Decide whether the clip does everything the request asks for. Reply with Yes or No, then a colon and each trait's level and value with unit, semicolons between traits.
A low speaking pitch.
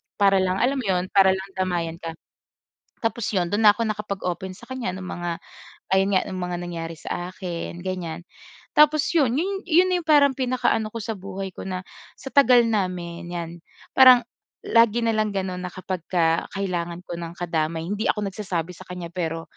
No: high, 190 Hz